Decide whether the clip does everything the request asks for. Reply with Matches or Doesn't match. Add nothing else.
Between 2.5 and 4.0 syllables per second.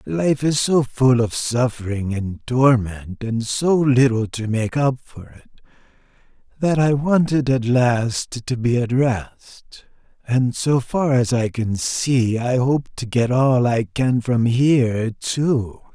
Matches